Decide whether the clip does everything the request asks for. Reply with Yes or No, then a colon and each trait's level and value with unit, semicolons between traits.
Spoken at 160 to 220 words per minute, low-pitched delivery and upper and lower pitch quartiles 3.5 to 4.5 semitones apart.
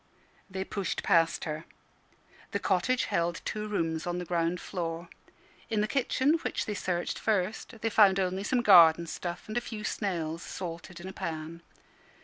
No: average, 165 wpm; medium, 180 Hz; average, 3.9 semitones